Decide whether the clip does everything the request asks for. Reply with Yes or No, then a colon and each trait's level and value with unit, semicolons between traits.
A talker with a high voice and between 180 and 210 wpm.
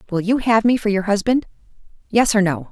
Yes: high, 210 Hz; average, 200 wpm